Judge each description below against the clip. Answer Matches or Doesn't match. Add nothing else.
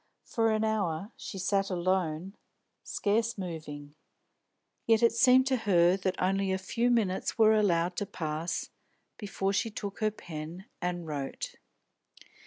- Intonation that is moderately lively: Matches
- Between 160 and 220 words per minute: Doesn't match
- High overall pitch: Matches